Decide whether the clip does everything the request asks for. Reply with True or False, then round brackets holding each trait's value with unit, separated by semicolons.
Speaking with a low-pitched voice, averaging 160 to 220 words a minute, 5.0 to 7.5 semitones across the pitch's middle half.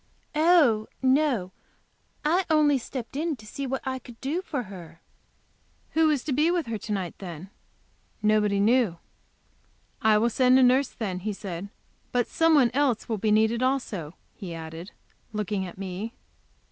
False (230 Hz; 165 wpm; 5.5 semitones)